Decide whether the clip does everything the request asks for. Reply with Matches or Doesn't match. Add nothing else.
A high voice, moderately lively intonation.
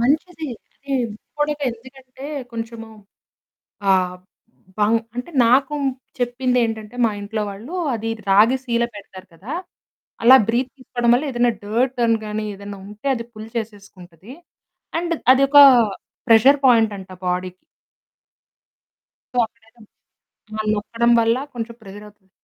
Matches